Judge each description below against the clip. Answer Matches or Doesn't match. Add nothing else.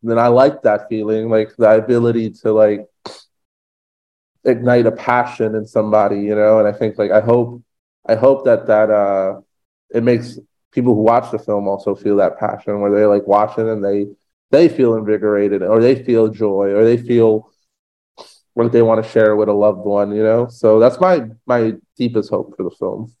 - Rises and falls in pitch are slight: Matches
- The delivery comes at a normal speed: Matches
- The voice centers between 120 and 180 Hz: Doesn't match